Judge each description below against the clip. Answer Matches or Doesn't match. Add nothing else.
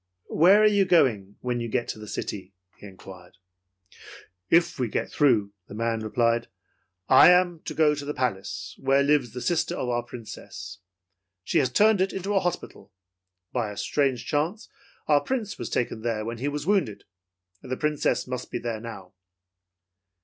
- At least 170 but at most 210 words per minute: Matches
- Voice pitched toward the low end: Matches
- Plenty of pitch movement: Matches